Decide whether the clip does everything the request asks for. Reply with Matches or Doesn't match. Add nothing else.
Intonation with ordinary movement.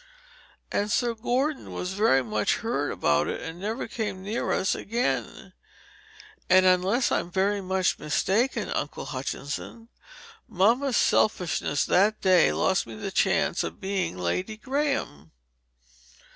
Doesn't match